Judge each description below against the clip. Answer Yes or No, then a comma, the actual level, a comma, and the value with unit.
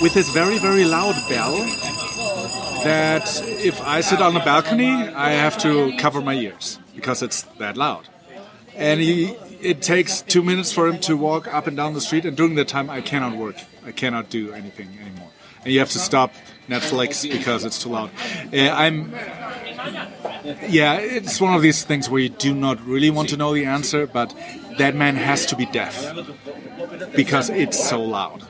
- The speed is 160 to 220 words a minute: Yes, average, 185 wpm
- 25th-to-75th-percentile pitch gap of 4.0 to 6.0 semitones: Yes, average, 4.4 semitones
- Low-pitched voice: No, medium, 150 Hz